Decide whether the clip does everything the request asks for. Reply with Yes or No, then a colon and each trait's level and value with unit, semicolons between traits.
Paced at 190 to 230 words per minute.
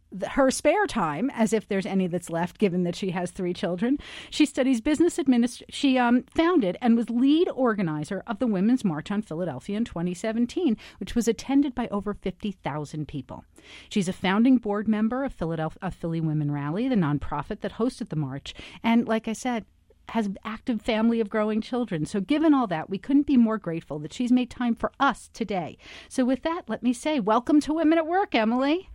Yes: average, 200 wpm